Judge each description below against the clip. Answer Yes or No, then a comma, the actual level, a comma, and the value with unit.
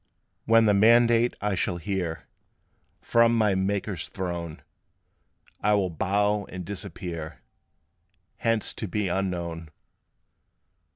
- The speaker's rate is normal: No, slow, 105 wpm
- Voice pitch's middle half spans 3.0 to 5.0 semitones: Yes, average, 3.4 semitones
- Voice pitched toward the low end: Yes, low, 100 Hz